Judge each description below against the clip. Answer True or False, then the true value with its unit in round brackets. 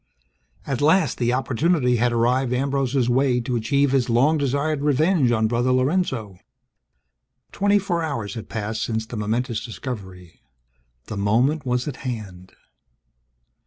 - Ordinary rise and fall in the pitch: True (3.8 semitones)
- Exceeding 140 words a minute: False (135 wpm)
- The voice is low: True (125 Hz)